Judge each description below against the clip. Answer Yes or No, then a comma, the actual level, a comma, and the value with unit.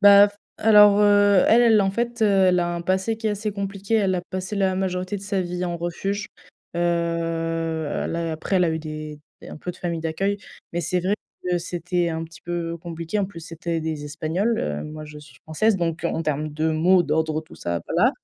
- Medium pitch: Yes, medium, 175 Hz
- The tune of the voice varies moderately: Yes, average, 3.5 semitones